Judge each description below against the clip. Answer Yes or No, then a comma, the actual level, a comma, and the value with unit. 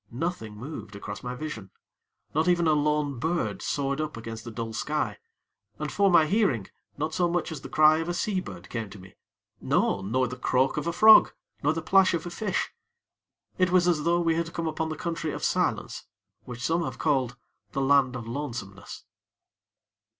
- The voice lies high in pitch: No, medium, 150 Hz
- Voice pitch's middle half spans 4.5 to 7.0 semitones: Yes, wide, 5.6 semitones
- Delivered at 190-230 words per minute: Yes, average, 195 wpm